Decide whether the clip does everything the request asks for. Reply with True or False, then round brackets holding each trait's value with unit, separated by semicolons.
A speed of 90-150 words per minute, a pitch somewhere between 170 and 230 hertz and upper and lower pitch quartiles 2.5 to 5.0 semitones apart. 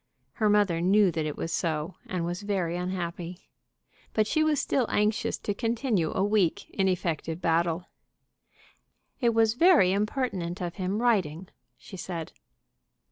True (140 wpm; 185 Hz; 3.9 semitones)